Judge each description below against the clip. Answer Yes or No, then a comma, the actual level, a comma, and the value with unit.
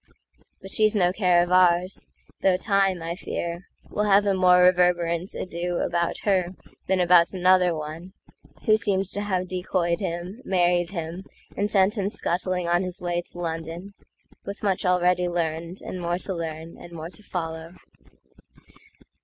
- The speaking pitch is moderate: Yes, medium, 180 Hz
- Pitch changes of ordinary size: No, narrow, 1.8 semitones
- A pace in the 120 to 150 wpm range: Yes, average, 140 wpm